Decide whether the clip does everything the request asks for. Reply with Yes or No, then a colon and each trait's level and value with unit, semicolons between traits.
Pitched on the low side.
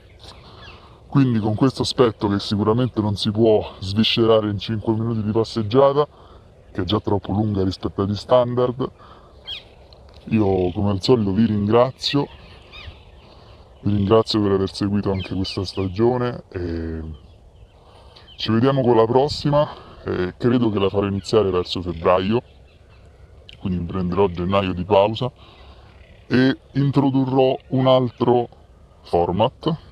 Yes: low, 105 Hz